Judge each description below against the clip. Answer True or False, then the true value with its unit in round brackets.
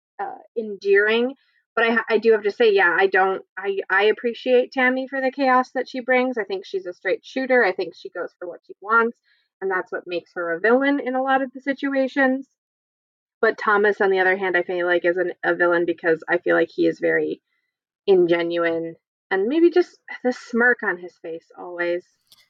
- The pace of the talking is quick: True (210 wpm)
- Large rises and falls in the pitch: True (6.6 semitones)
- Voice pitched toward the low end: False (225 Hz)